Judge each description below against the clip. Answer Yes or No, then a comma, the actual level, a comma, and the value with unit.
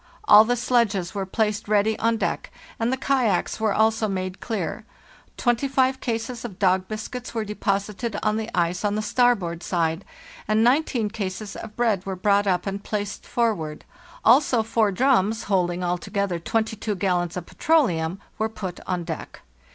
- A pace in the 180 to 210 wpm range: No, average, 160 wpm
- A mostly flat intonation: No, average, 3.4 semitones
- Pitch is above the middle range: Yes, high, 210 Hz